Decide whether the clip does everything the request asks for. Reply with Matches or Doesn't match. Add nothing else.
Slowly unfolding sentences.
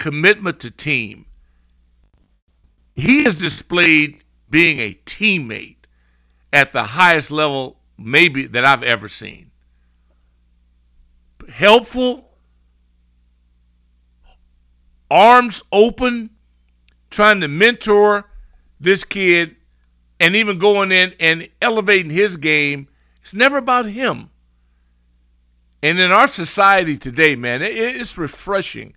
Matches